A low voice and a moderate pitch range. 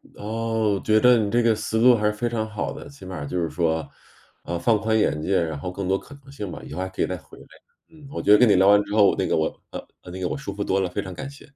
Yes: low, 105 Hz; average, 3.5 semitones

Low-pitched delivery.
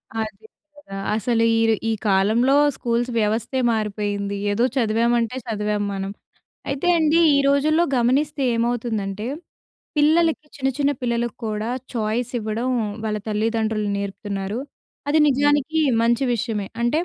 No: high, 230 Hz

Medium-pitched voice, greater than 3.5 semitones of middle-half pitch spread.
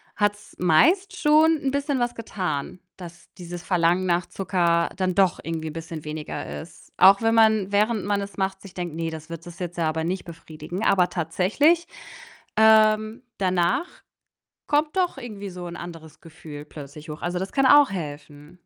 Yes: medium, 180 Hz; average, 4.7 semitones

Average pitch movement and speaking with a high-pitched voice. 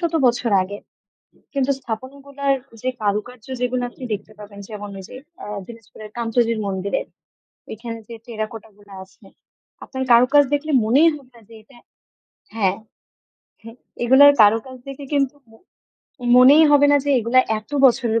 Yes: average, 3.9 semitones; high, 240 Hz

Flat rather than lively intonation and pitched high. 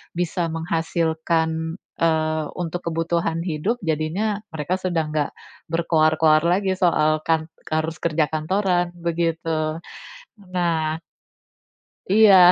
No: narrow, 1.8 semitones; medium, 165 Hz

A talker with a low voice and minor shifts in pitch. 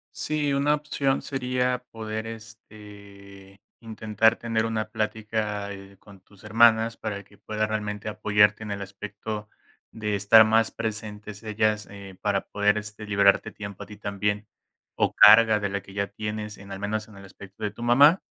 Yes: low, 105 Hz; narrow, 1.6 semitones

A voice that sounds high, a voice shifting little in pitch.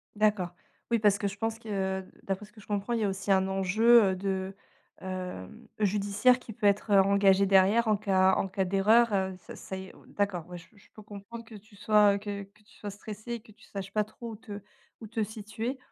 Yes: high, 205 Hz; narrow, 2.0 semitones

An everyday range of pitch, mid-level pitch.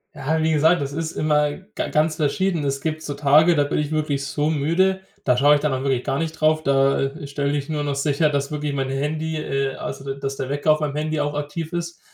No: narrow, 2.1 semitones; medium, 150 Hz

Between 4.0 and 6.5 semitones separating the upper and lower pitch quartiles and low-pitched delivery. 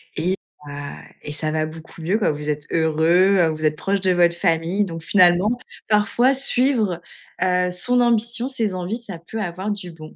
No: average, 4.4 semitones; medium, 180 Hz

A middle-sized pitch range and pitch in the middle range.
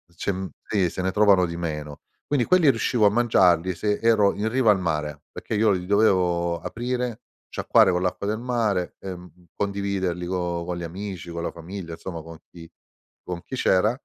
No: average, 3.8 semitones; very low, 95 Hz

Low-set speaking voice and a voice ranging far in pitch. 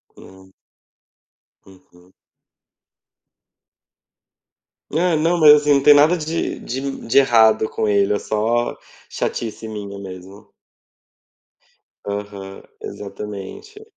Yes: low, 110 Hz; wide, 6.8 semitones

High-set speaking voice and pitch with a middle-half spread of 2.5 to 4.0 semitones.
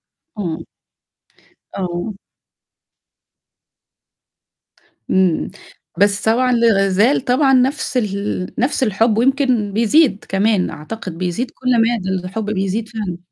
No: high, 215 Hz; average, 4.6 semitones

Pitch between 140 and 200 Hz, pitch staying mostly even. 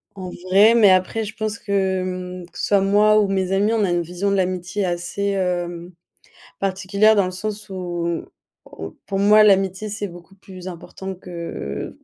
Yes: high, 190 Hz; narrow, 2.3 semitones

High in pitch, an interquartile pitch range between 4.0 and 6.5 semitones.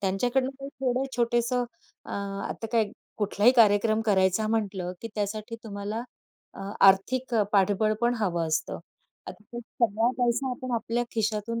No: high, 225 Hz; average, 2.8 semitones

